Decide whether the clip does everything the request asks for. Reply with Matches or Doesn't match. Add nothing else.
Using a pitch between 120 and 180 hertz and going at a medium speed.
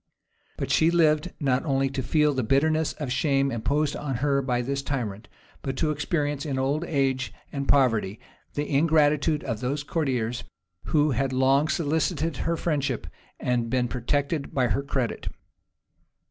Matches